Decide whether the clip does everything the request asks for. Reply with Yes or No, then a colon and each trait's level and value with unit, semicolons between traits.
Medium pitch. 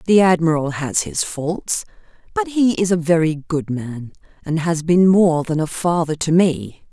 Yes: medium, 165 Hz